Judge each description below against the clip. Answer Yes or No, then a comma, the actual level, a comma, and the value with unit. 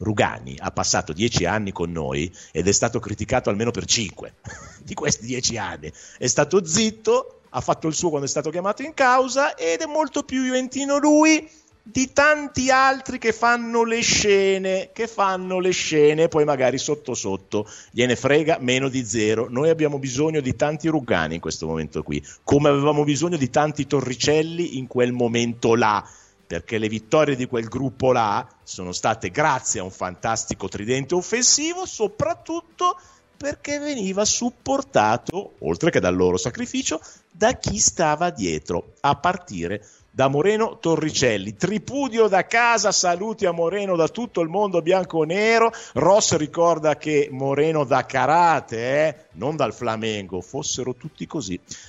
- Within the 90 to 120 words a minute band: No, average, 155 wpm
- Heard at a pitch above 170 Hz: No, medium, 150 Hz